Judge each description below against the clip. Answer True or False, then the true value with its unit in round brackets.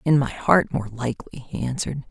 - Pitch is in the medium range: False (130 Hz)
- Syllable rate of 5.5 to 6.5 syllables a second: True (5.6 syllables/s)